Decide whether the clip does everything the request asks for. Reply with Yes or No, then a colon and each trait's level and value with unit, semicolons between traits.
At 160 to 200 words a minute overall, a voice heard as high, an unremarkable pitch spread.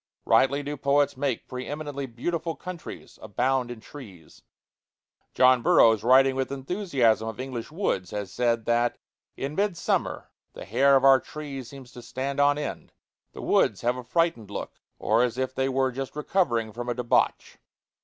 No: average, 165 wpm; low, 130 Hz; average, 3.2 semitones